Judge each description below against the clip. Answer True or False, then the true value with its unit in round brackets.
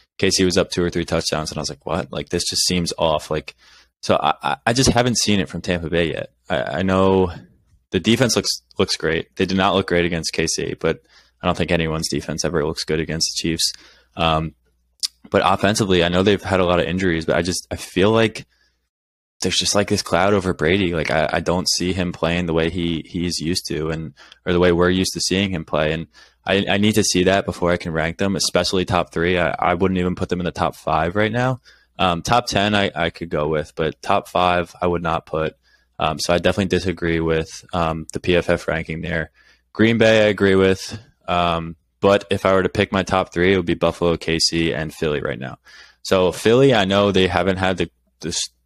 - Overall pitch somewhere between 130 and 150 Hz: False (90 Hz)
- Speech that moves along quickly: True (235 wpm)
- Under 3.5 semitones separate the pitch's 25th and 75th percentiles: True (2.6 semitones)